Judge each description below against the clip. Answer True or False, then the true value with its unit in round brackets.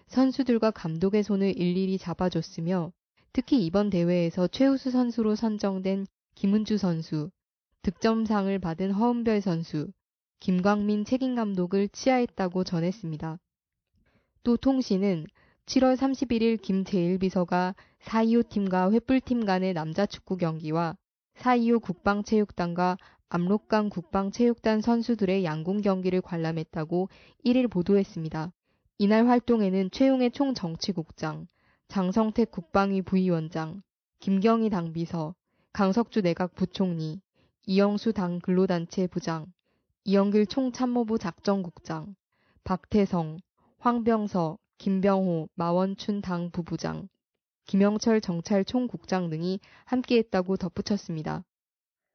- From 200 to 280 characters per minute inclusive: True (260 characters per minute)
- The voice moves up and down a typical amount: True (3.9 semitones)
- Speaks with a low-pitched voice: False (195 Hz)